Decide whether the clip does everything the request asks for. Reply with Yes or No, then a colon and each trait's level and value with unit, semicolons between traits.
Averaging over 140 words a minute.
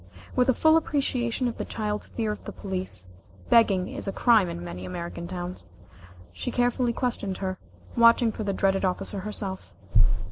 Yes: average, 170 wpm